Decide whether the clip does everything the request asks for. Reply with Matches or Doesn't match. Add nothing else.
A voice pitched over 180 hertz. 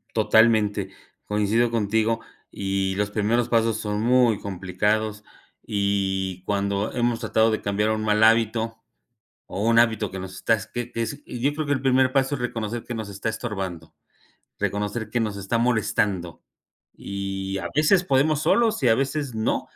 Doesn't match